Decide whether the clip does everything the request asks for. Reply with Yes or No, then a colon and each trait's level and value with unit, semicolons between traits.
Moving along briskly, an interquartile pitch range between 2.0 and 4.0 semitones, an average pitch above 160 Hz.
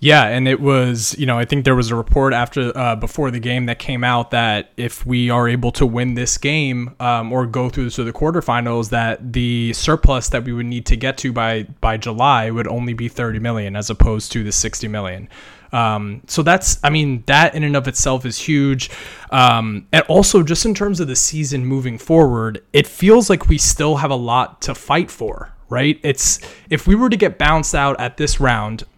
No: fast, 220 wpm; average, 3.4 semitones; low, 125 Hz